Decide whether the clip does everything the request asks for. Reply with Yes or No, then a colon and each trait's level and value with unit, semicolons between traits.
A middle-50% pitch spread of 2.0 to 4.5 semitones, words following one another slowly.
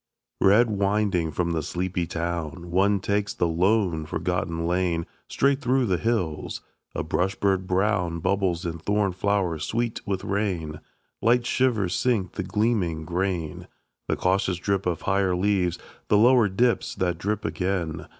No: average, 3.2 semitones; average, 150 wpm